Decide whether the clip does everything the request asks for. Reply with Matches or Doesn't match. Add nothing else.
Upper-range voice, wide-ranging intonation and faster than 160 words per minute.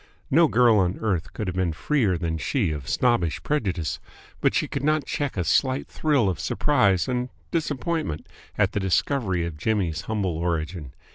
Doesn't match